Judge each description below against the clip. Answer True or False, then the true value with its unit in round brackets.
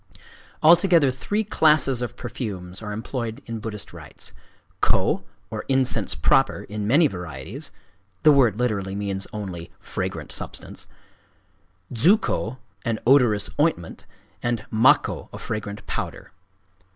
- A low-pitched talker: True (110 Hz)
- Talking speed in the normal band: False (110 wpm)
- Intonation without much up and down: False (4.9 semitones)